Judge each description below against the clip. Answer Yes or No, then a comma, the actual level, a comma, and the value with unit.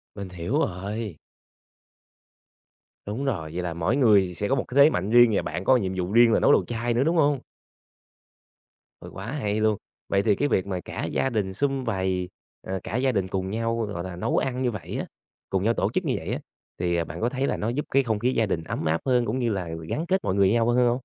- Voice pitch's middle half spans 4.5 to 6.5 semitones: Yes, average, 5.0 semitones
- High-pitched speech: No, low, 110 Hz